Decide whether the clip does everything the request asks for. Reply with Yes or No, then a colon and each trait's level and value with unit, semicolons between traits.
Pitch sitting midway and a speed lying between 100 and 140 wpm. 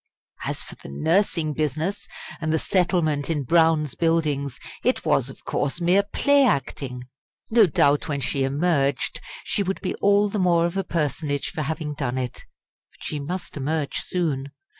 No: medium, 155 Hz; average, 165 wpm